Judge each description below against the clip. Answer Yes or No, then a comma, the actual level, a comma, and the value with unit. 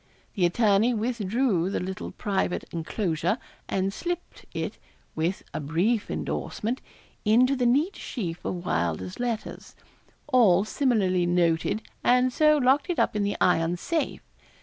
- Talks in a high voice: Yes, high, 205 Hz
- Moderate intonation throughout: No, wide, 6.0 semitones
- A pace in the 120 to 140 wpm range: Yes, slow, 135 wpm